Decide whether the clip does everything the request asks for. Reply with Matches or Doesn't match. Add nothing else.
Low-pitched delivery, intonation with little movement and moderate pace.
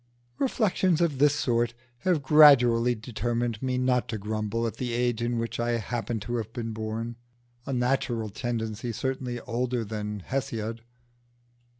Matches